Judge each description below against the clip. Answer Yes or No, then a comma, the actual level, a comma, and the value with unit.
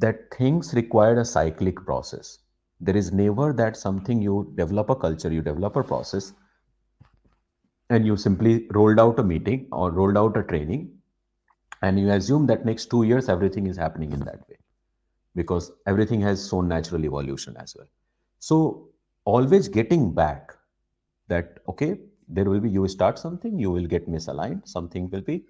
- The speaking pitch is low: Yes, low, 100 Hz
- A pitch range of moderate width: Yes, average, 4.5 semitones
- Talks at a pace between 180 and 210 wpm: No, average, 165 wpm